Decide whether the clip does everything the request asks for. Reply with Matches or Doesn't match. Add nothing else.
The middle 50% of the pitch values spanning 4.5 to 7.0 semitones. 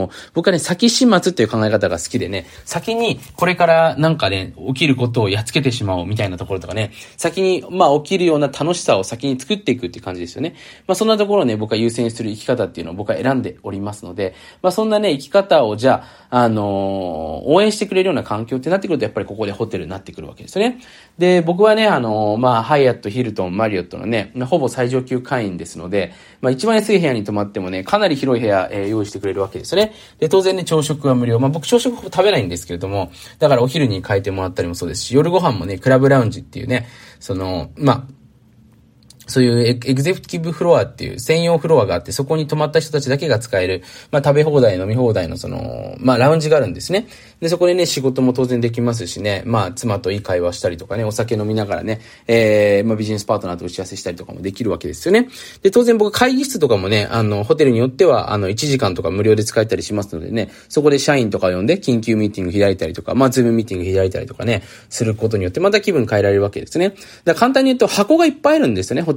Doesn't match